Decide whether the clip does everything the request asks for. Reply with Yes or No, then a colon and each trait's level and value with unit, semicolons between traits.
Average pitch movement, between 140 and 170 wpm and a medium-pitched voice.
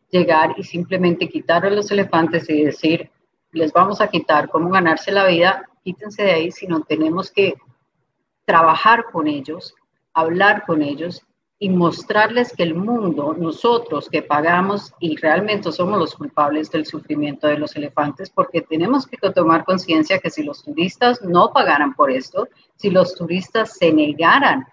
Yes: average, 3.5 semitones; average, 160 wpm; medium, 170 Hz